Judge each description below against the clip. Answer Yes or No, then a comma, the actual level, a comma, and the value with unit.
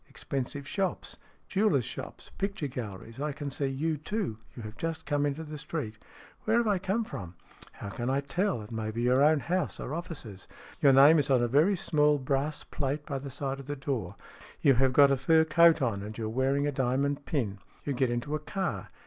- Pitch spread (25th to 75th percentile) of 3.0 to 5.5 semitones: Yes, average, 3.8 semitones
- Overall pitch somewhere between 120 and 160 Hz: Yes, medium, 140 Hz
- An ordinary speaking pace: No, fast, 225 wpm